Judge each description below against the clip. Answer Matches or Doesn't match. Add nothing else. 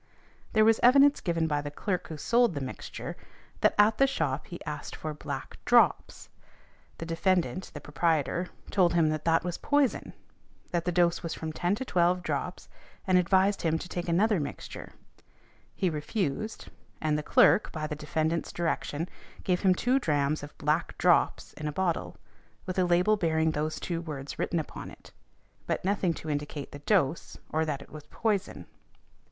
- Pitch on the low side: Doesn't match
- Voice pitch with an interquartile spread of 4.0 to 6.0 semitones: Doesn't match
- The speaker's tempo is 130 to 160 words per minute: Doesn't match